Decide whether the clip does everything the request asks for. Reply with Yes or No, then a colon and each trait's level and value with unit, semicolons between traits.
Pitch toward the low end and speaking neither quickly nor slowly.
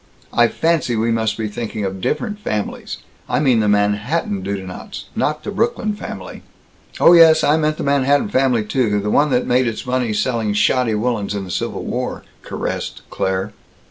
Yes: low, 120 Hz; average, 175 wpm